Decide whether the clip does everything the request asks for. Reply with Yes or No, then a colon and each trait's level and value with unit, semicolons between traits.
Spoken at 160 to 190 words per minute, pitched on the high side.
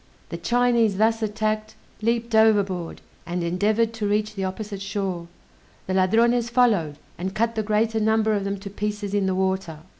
Yes: average, 170 wpm; high, 210 Hz